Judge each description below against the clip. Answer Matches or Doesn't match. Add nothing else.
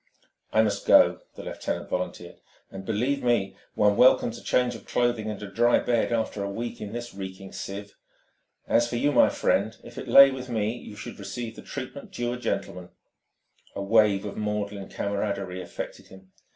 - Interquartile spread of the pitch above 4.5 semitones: Doesn't match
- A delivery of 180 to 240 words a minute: Matches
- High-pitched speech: Doesn't match